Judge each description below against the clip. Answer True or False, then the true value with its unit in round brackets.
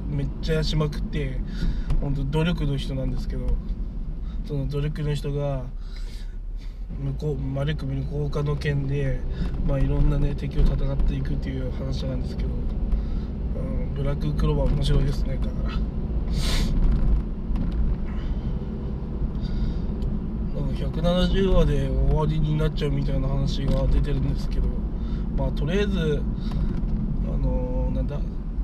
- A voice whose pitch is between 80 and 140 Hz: True (135 Hz)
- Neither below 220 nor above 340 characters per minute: True (270 characters per minute)